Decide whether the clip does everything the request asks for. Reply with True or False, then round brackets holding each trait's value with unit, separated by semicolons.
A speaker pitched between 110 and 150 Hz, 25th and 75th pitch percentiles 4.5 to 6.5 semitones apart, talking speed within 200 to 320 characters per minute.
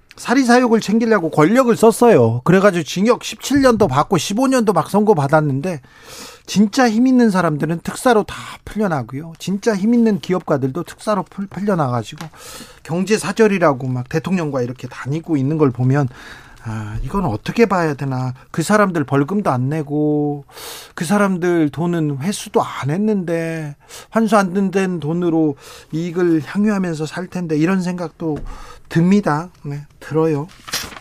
False (170 Hz; 5.6 semitones; 305 characters per minute)